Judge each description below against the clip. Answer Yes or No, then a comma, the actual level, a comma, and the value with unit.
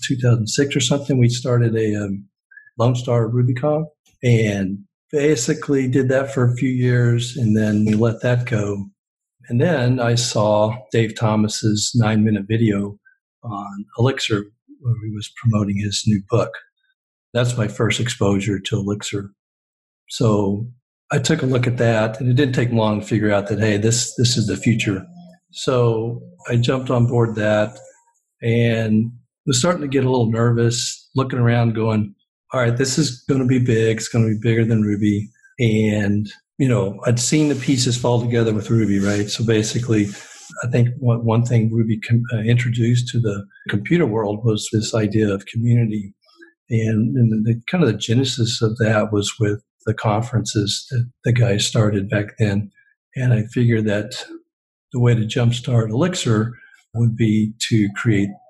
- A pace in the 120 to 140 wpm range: No, average, 165 wpm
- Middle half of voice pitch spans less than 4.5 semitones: Yes, average, 2.7 semitones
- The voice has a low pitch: Yes, low, 115 Hz